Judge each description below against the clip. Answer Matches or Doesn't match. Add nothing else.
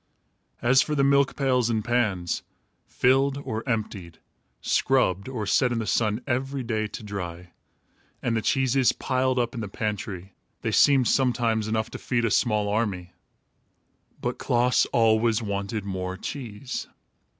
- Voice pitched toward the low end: Matches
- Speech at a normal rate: Matches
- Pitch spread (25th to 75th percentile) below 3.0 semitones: Doesn't match